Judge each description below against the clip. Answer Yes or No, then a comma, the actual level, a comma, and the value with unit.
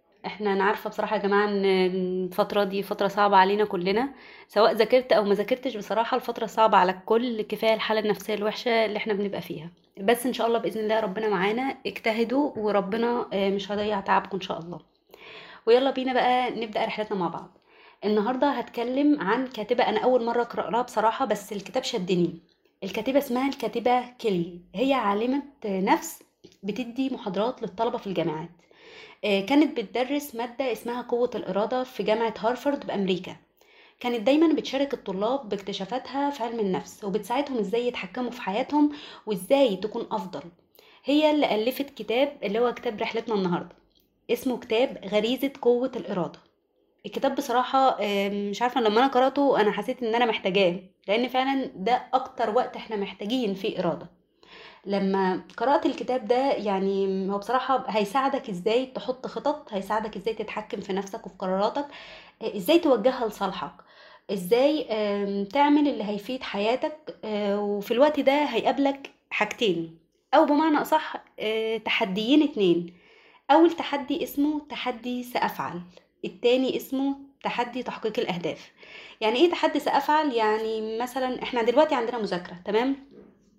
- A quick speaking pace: Yes, fast, 140 wpm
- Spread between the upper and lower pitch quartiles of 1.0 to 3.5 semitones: No, average, 4.1 semitones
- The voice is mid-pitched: No, high, 230 Hz